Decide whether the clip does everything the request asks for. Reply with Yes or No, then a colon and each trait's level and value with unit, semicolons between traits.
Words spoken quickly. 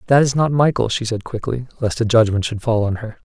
Yes: fast, 255 wpm